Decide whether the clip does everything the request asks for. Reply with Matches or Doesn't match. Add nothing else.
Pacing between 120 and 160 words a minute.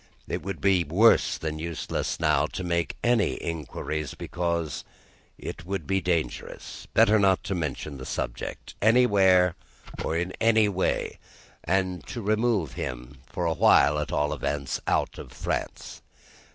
Matches